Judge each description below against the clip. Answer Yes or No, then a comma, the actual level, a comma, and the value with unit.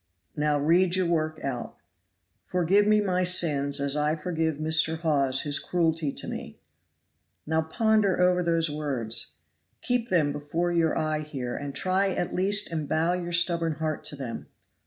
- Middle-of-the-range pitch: Yes, medium, 160 Hz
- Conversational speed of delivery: Yes, average, 160 wpm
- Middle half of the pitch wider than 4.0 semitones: No, average, 3.3 semitones